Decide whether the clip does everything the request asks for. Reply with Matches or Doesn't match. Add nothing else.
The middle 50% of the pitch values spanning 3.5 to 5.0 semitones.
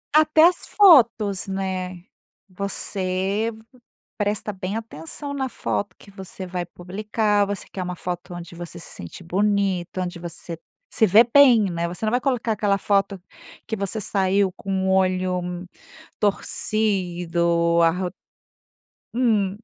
Doesn't match